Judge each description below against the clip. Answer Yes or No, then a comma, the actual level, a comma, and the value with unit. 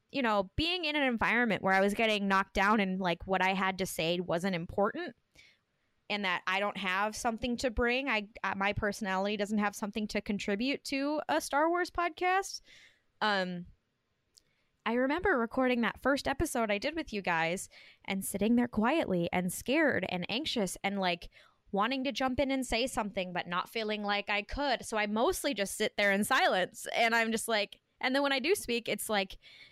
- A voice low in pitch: No, high, 215 Hz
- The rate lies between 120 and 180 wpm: No, average, 200 wpm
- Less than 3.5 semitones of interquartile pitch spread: No, average, 5.1 semitones